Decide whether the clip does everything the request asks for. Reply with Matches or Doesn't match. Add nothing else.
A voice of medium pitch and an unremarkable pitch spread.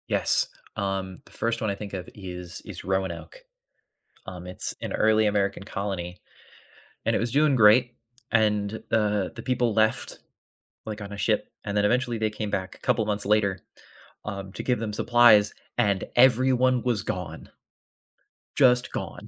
Doesn't match